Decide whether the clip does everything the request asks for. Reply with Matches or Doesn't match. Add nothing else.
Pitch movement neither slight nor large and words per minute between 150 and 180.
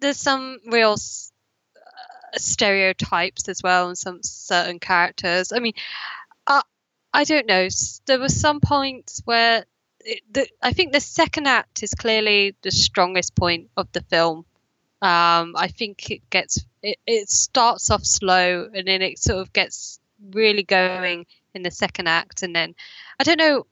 Doesn't match